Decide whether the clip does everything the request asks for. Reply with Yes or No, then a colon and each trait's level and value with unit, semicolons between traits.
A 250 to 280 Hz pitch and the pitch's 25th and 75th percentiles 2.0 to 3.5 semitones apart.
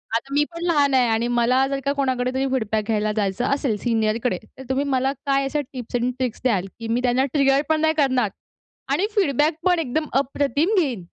Yes: very high, 260 Hz; average, 3.1 semitones